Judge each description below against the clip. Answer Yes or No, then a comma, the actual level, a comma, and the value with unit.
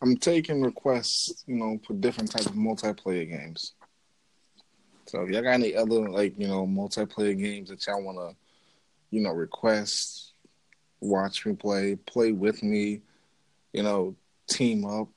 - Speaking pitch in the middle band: No, low, 105 Hz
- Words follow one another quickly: No, average, 150 wpm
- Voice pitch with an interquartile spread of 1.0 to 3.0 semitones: Yes, narrow, 2.5 semitones